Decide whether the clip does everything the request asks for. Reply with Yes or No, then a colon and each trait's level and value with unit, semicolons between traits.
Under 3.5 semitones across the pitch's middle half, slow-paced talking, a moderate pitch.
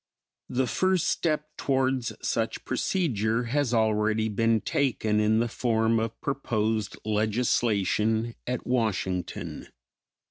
No: average, 2.8 semitones; slow, 105 wpm; low, 115 Hz